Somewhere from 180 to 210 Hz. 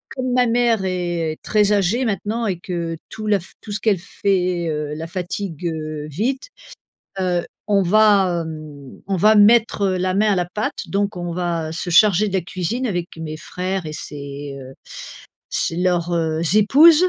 Yes: medium, 185 Hz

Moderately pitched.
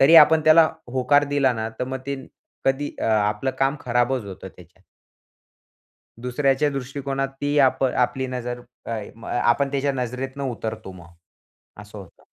No: low, 130 Hz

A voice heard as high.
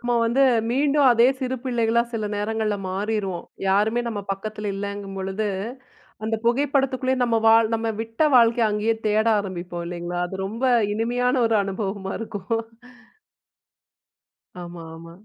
Yes: high, 220 Hz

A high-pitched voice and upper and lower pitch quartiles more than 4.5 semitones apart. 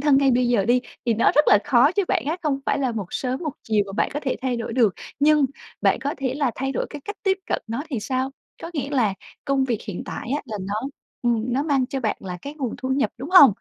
No: very high, 260 Hz; average, 3.5 semitones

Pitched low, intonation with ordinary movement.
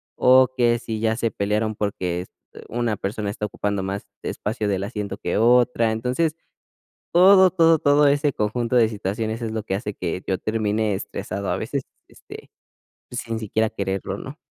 Yes: low, 110 Hz; average, 3.2 semitones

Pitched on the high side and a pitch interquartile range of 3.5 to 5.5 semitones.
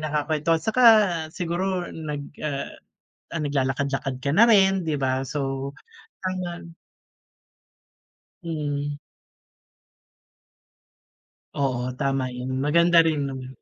No: medium, 150 Hz; average, 3.8 semitones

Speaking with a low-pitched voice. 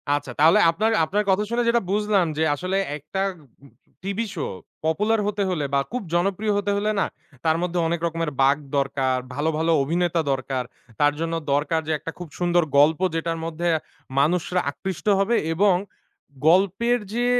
No: medium, 175 Hz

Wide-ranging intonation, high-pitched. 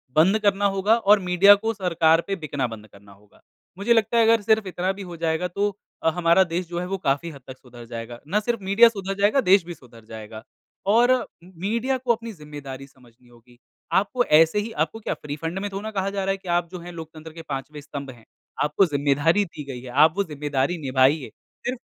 No: wide, 6.5 semitones; medium, 170 Hz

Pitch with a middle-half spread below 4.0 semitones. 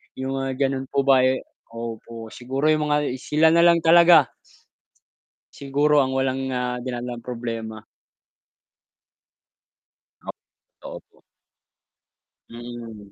Yes: average, 3.6 semitones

